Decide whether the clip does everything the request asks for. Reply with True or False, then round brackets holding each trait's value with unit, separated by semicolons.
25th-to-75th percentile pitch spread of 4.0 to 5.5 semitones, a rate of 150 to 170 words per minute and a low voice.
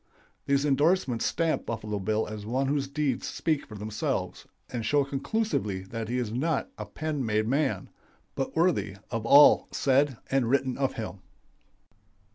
True (4.7 semitones; 155 wpm; 130 Hz)